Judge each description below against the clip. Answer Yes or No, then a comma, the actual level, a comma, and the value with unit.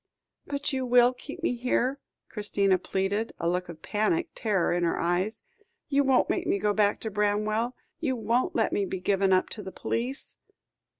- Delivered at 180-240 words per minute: Yes, average, 185 wpm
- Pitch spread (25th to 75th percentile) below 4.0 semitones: No, average, 4.6 semitones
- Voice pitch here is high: Yes, high, 215 Hz